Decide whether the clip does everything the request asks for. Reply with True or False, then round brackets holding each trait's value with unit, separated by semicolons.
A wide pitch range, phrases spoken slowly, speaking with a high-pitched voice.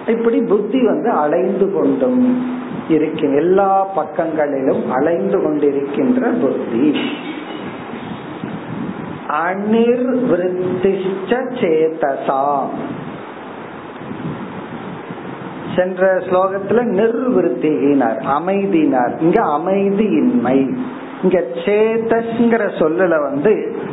True (5.9 semitones; 55 wpm; 195 Hz)